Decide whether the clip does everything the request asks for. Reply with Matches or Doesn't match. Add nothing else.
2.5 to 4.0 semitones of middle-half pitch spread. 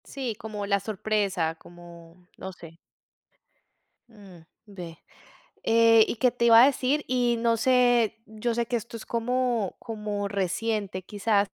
Matches